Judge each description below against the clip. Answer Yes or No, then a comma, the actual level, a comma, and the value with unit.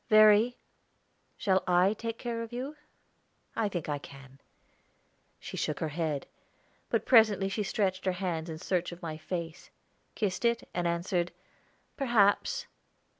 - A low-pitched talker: No, high, 190 Hz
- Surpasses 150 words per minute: No, average, 140 wpm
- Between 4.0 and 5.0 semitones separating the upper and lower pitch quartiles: Yes, average, 4.6 semitones